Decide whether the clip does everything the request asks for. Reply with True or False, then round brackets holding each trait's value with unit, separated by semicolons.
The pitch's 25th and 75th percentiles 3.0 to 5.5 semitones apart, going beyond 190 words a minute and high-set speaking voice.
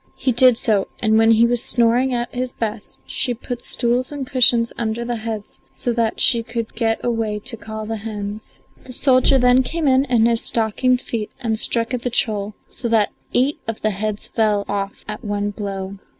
False (2.4 semitones; 200 wpm; 230 Hz)